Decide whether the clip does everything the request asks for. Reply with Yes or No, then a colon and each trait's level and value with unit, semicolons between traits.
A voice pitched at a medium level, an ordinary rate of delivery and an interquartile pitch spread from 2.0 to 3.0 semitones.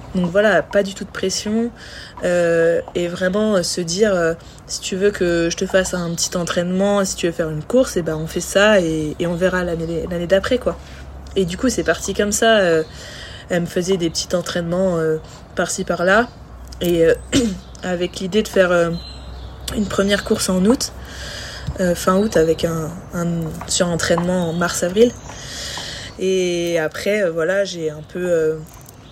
Yes: medium, 180 Hz; average, 185 wpm; average, 2.7 semitones